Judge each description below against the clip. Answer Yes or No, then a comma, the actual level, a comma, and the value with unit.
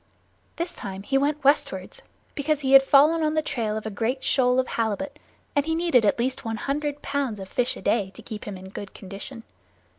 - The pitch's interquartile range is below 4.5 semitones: No, average, 4.9 semitones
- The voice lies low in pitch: No, very high, 260 Hz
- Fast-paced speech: Yes, fast, 215 wpm